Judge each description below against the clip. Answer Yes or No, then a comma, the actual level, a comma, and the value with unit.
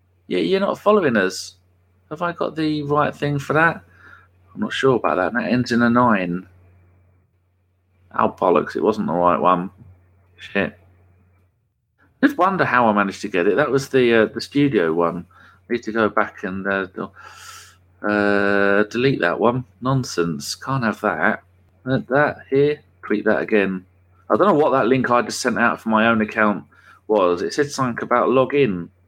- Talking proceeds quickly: No, average, 180 wpm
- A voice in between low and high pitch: No, low, 105 Hz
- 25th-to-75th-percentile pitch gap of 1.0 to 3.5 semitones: No, average, 5.1 semitones